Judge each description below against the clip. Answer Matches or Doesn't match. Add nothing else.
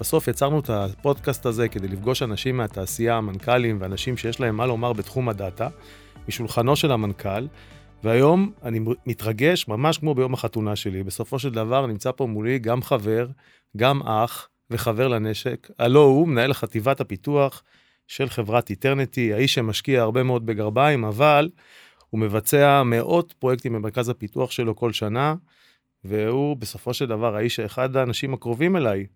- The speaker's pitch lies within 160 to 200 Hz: Doesn't match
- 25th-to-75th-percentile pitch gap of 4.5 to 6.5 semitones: Doesn't match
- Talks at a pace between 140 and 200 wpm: Matches